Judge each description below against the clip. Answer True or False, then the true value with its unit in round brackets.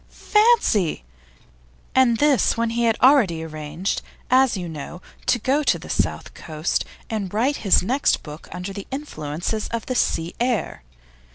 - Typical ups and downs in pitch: False (7.2 semitones)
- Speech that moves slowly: False (155 wpm)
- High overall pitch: True (220 Hz)